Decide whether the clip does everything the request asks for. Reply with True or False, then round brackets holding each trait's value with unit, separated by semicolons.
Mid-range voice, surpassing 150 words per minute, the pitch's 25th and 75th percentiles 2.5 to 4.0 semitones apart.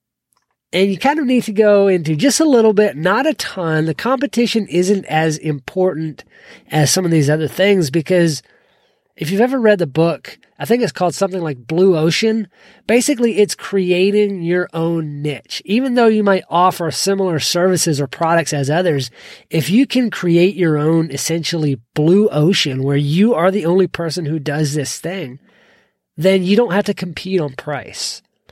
False (180 Hz; 180 wpm; 4.5 semitones)